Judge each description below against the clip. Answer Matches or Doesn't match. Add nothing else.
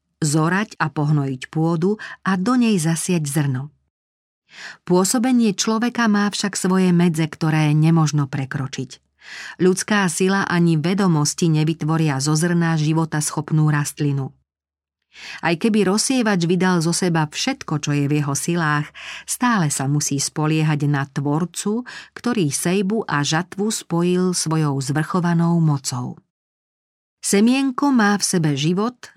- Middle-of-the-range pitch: Matches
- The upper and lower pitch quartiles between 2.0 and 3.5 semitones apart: Doesn't match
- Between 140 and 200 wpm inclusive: Doesn't match